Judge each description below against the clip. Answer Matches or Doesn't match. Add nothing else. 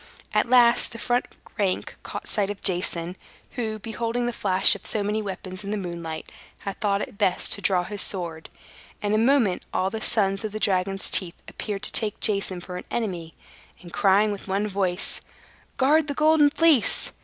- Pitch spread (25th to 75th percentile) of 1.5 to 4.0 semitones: Matches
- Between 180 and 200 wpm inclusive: Matches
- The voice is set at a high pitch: Matches